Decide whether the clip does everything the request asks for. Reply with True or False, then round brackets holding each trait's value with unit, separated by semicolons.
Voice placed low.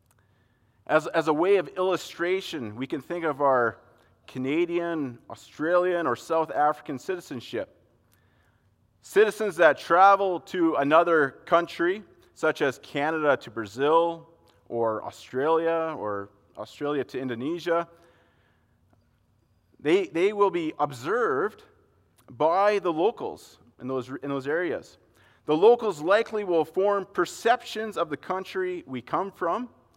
False (165 Hz)